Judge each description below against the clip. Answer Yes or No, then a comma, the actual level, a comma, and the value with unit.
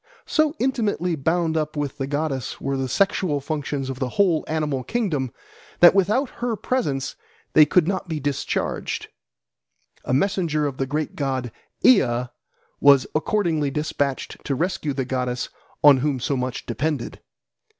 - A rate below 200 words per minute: Yes, average, 150 wpm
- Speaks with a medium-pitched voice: Yes, medium, 150 Hz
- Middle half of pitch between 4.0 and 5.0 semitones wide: Yes, average, 4.6 semitones